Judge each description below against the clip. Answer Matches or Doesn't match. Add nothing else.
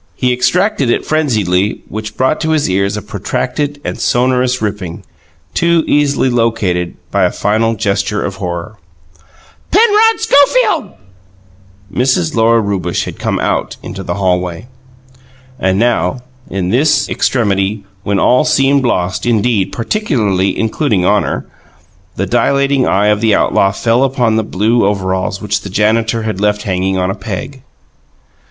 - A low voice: Matches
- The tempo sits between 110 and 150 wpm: Matches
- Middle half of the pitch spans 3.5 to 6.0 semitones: Matches